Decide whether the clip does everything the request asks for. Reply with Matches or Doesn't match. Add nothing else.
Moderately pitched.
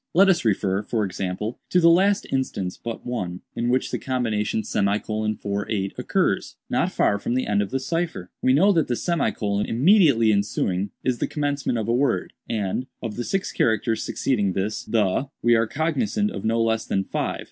Doesn't match